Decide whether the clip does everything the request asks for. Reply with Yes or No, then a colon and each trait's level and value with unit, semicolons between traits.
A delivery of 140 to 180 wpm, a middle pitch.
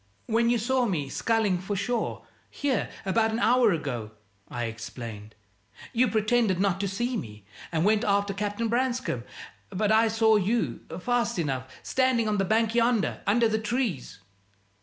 No: average, 160 wpm; high, 215 Hz